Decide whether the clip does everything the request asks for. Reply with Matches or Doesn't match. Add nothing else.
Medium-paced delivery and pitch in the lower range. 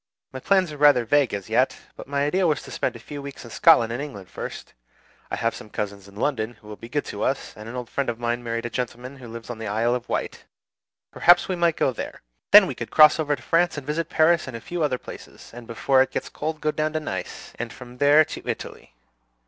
Doesn't match